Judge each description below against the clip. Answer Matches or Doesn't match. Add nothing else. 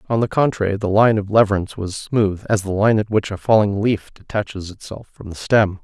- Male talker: Matches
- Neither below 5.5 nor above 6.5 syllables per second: Matches